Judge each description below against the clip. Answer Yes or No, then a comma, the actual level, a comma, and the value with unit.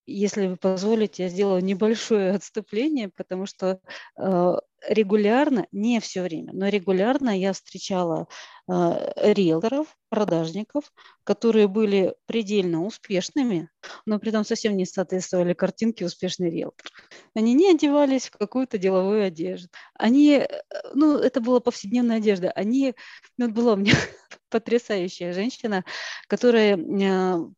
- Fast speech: No, average, 120 wpm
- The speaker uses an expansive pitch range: No, average, 4.0 semitones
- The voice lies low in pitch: No, high, 205 Hz